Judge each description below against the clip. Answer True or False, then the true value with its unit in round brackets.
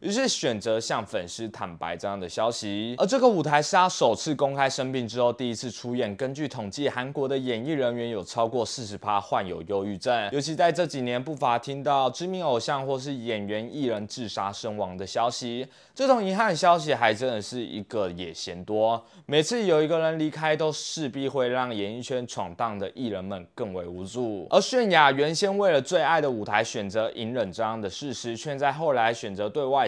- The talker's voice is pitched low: True (125 Hz)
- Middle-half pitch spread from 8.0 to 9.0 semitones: False (5.5 semitones)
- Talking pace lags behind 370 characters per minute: True (305 characters per minute)